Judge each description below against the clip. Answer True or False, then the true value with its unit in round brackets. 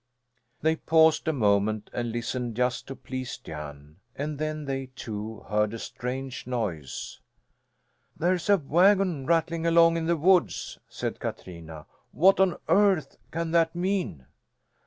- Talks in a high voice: False (140 Hz)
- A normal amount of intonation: False (7.3 semitones)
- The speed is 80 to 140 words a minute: True (135 wpm)